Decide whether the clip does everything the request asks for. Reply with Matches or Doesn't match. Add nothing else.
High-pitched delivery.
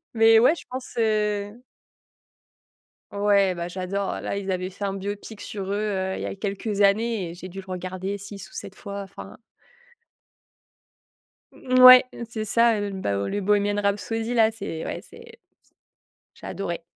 Matches